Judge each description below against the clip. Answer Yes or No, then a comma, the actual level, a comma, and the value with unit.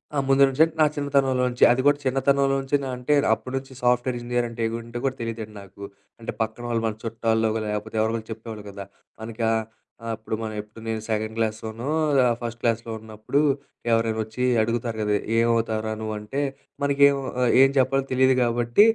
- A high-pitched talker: No, low, 115 Hz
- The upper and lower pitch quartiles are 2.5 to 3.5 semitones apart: Yes, average, 2.9 semitones